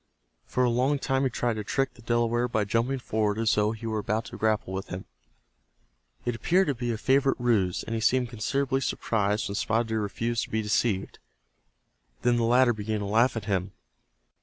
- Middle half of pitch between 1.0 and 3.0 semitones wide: Yes, narrow, 2.5 semitones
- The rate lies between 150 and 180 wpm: No, fast, 205 wpm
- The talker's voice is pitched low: Yes, low, 115 Hz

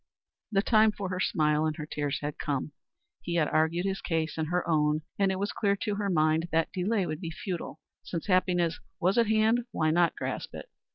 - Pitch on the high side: No, medium, 175 Hz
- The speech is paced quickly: Yes, fast, 215 wpm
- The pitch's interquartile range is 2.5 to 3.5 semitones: No, average, 3.9 semitones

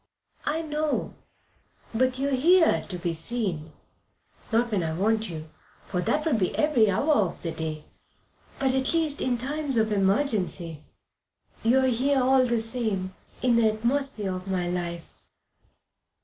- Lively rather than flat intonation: Yes, wide, 6.4 semitones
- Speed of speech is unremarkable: Yes, average, 155 wpm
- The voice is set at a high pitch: Yes, high, 225 Hz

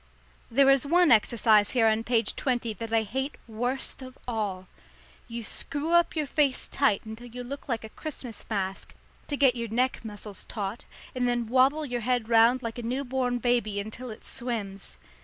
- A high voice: Yes, high, 240 Hz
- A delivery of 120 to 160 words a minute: No, average, 185 wpm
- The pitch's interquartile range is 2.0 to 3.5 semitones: Yes, average, 2.9 semitones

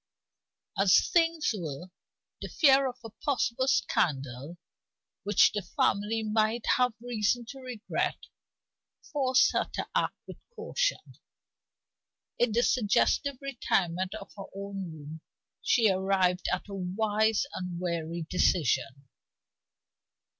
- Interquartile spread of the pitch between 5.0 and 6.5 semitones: Yes, wide, 5.4 semitones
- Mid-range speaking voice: No, high, 205 Hz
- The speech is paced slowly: Yes, slow, 115 wpm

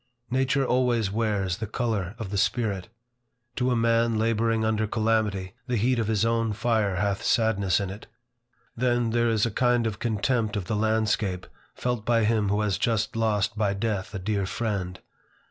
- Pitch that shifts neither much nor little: No, narrow, 2.3 semitones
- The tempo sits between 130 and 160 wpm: No, average, 180 wpm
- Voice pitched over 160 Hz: No, low, 110 Hz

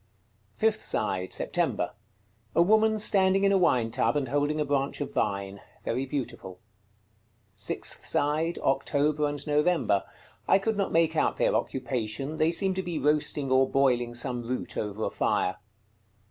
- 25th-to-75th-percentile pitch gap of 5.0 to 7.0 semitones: Yes, wide, 5.5 semitones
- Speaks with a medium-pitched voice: Yes, medium, 145 Hz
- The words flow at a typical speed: Yes, average, 155 wpm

